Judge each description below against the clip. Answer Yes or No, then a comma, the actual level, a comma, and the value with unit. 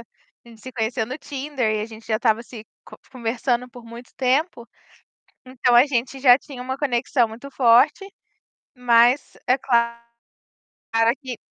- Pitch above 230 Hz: Yes, high, 245 Hz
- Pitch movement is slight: Yes, narrow, 1.9 semitones